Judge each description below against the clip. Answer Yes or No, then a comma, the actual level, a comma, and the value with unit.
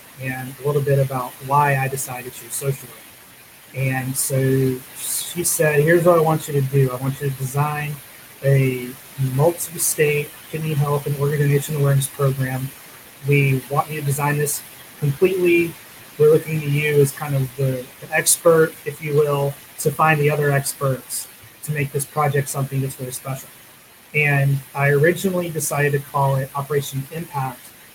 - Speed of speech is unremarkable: Yes, average, 170 wpm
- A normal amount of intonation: No, narrow, 2.0 semitones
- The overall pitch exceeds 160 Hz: No, medium, 140 Hz